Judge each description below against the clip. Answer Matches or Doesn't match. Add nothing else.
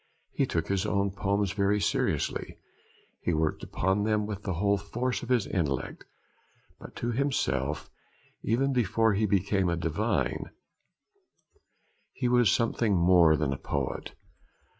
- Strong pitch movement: Doesn't match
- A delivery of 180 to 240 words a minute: Doesn't match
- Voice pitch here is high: Doesn't match